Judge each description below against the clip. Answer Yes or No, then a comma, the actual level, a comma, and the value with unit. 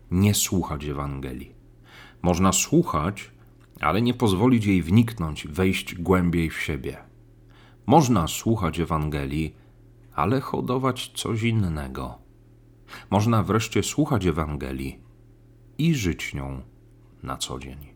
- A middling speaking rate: No, slow, 105 wpm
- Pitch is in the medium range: No, low, 100 Hz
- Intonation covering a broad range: Yes, wide, 7.5 semitones